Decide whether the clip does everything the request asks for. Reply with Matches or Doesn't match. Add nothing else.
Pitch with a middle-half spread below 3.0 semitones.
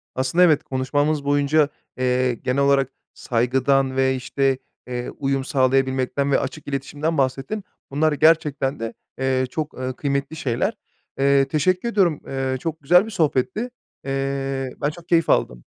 Matches